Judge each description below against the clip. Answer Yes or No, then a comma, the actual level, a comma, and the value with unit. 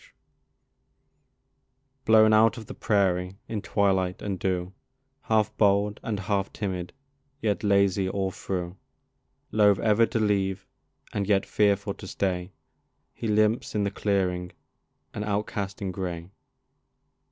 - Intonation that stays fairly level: Yes, narrow, 2.0 semitones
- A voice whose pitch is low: Yes, low, 100 Hz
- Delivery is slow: Yes, slow, 130 wpm